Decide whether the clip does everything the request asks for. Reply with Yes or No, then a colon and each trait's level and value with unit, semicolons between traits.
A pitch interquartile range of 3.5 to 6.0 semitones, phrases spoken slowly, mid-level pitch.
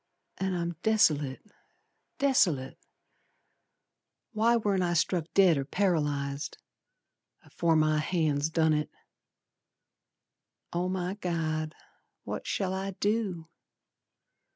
Yes: average, 3.8 semitones; slow, 95 wpm; medium, 170 Hz